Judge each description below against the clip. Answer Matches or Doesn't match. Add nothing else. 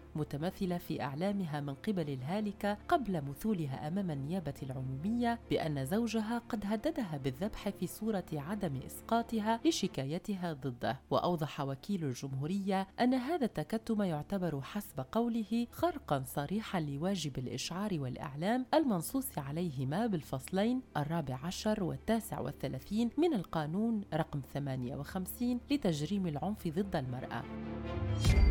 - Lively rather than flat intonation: Matches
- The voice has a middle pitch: Matches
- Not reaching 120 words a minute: Matches